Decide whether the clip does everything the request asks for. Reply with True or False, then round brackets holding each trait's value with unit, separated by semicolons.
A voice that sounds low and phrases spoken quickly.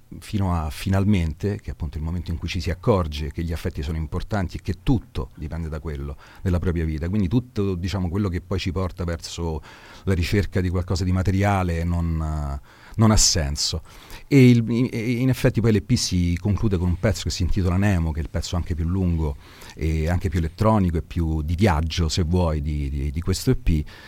True (90 Hz; 210 wpm)